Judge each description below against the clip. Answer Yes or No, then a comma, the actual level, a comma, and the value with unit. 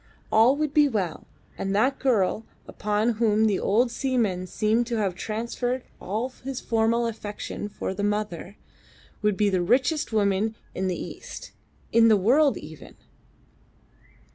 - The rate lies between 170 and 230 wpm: No, average, 145 wpm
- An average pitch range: Yes, average, 3.2 semitones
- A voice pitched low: No, high, 220 Hz